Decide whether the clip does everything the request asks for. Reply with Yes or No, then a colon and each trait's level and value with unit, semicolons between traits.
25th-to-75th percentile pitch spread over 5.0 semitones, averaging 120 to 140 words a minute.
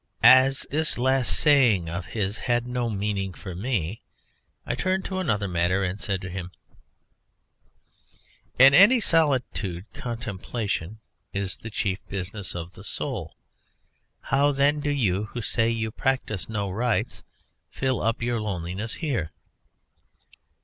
Yes: wide, 5.5 semitones; slow, 135 wpm